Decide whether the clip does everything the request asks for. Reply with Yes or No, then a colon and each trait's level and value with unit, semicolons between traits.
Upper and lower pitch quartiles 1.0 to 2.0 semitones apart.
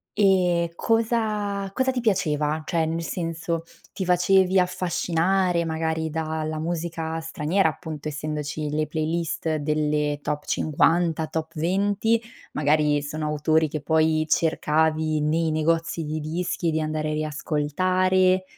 No: average, 2.7 semitones